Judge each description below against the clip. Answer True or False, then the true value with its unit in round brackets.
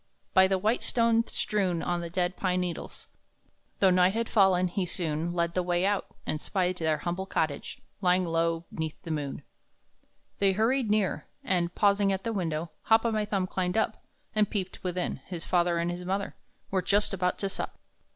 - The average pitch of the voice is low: False (185 Hz)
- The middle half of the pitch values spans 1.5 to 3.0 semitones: True (2.5 semitones)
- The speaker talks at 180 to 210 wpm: True (185 wpm)